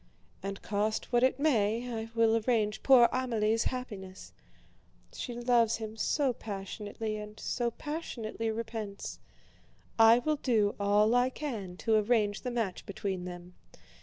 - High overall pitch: Yes, high, 225 Hz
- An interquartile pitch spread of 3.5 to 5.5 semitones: No, average, 2.7 semitones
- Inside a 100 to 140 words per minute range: Yes, slow, 135 wpm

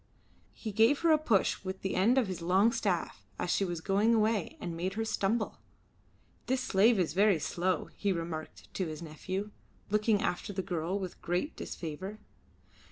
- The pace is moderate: Yes, average, 175 wpm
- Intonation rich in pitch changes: No, average, 3.7 semitones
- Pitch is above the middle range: Yes, high, 195 Hz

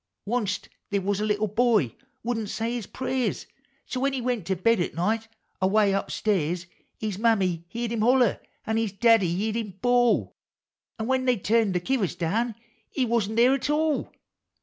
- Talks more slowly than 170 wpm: No, average, 185 wpm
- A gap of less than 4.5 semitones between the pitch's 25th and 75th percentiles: Yes, average, 3.6 semitones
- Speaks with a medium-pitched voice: No, high, 220 Hz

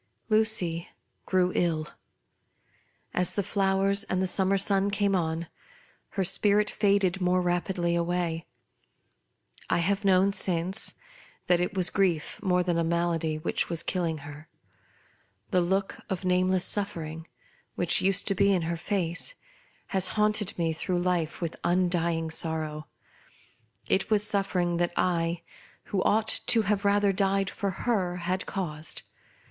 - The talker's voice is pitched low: No, medium, 180 Hz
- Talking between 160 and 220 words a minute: No, average, 140 wpm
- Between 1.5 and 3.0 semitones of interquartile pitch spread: Yes, narrow, 2.6 semitones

